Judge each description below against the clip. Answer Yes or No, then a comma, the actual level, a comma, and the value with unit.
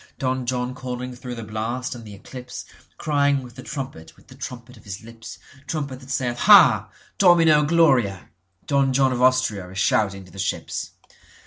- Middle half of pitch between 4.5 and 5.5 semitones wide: No, average, 3.7 semitones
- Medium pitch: No, low, 125 Hz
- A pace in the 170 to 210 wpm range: No, average, 150 wpm